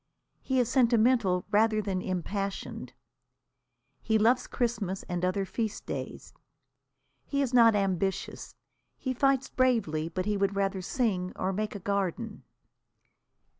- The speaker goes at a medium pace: No, slow, 130 wpm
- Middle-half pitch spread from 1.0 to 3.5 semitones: No, average, 4.0 semitones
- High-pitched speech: Yes, high, 205 Hz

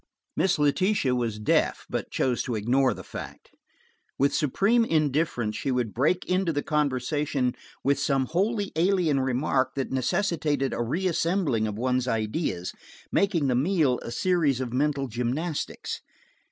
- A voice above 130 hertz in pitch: Yes, medium, 140 Hz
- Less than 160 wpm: Yes, average, 140 wpm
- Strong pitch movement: No, average, 4.9 semitones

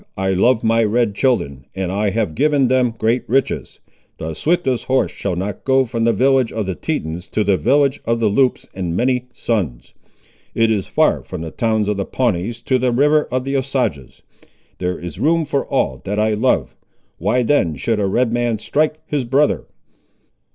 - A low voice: Yes, low, 115 Hz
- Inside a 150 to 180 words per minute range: No, average, 190 wpm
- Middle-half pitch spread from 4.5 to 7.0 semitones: Yes, average, 4.9 semitones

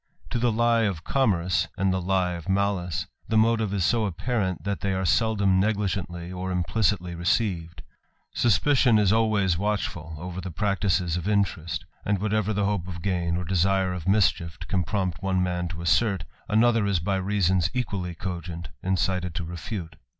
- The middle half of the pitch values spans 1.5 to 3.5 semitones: Yes, average, 3.0 semitones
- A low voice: Yes, very low, 95 Hz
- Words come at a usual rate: Yes, average, 170 wpm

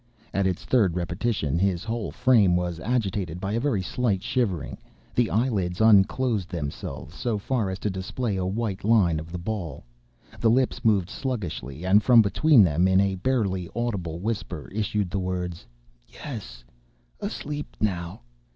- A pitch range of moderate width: Yes, average, 4.5 semitones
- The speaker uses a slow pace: No, average, 150 wpm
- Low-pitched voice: Yes, very low, 95 Hz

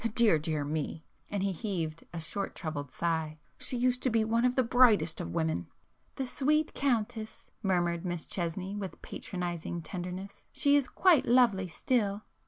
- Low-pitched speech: No, high, 190 Hz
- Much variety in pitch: Yes, wide, 6.4 semitones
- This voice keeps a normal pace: Yes, average, 155 wpm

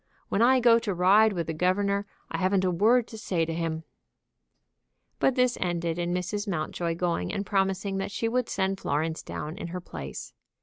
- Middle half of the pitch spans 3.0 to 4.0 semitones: Yes, average, 3.4 semitones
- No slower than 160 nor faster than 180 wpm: No, average, 190 wpm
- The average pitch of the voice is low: No, high, 190 Hz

